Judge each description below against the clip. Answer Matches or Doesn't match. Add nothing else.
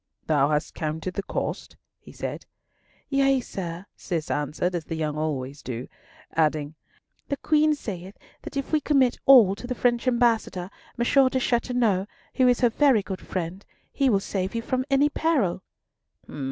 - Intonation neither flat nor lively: Doesn't match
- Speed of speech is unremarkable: Matches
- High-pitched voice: Matches